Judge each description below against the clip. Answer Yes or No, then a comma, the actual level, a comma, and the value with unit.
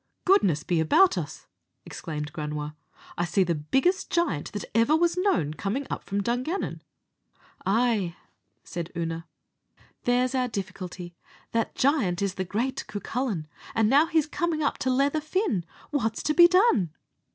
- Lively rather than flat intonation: Yes, wide, 8.7 semitones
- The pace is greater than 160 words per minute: No, average, 150 wpm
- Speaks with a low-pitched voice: No, high, 220 Hz